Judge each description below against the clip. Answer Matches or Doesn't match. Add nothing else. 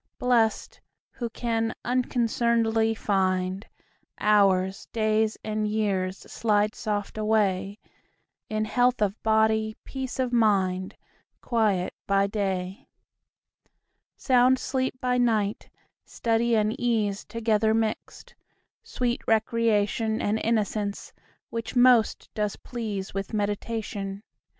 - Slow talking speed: Matches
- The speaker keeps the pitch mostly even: Matches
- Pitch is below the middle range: Doesn't match